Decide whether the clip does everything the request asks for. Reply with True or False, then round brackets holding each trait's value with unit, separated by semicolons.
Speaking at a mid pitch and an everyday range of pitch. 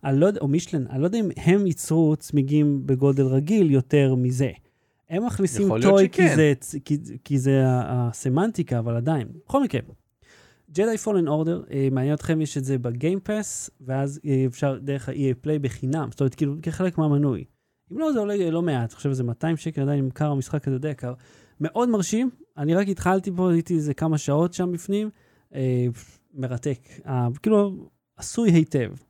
True (150 Hz; 5.0 semitones)